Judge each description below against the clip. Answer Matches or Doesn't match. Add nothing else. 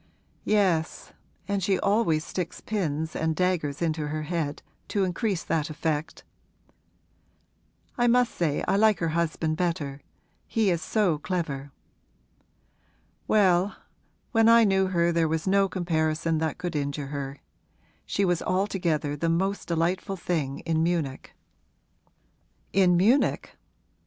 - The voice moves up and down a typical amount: Matches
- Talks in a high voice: Doesn't match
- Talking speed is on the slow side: Matches